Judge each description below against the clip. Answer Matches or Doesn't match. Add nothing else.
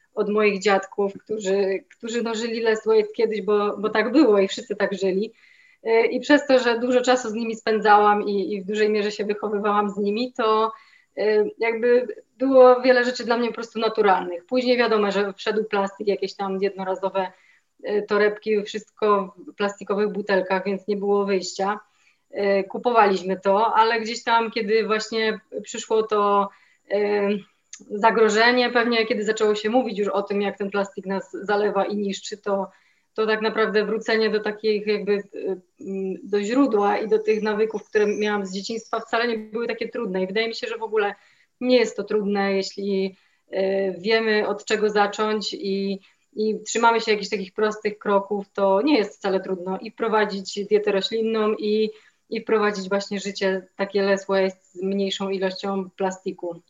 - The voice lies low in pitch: Doesn't match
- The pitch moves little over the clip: Matches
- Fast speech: Matches